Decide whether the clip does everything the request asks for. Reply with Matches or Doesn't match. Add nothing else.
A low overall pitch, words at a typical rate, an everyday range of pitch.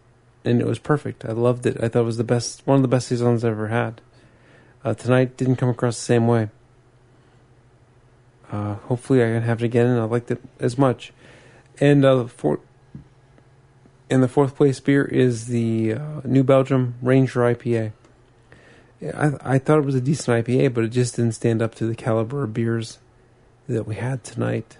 Doesn't match